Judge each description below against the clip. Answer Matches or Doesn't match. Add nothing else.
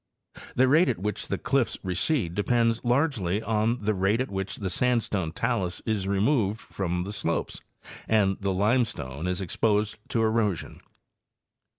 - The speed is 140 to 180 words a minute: Matches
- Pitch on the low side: Matches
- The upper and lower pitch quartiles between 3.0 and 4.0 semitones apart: Matches